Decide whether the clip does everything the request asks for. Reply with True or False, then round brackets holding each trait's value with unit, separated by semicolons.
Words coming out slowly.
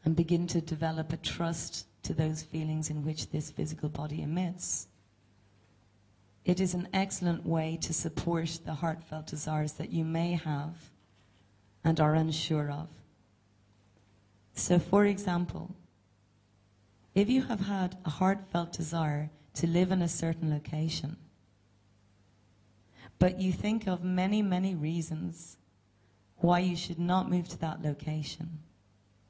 True (130 wpm)